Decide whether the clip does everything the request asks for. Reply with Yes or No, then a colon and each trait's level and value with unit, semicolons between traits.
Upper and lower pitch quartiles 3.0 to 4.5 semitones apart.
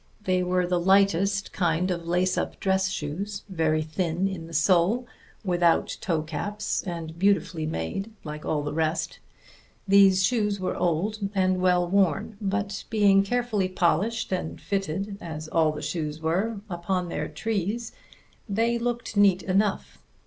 Yes: average, 3.3 semitones